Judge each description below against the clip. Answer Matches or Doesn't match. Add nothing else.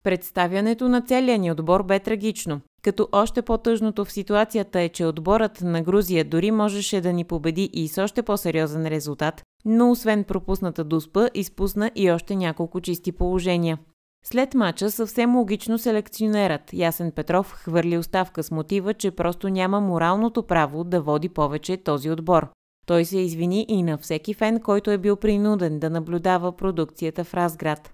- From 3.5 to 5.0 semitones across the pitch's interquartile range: Matches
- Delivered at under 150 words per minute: Doesn't match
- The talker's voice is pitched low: Doesn't match